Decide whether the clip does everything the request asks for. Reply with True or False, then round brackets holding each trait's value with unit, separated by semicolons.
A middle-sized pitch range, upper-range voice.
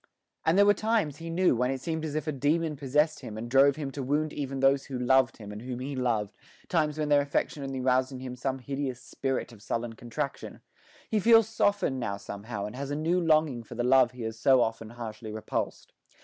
False (4.0 semitones; 135 Hz)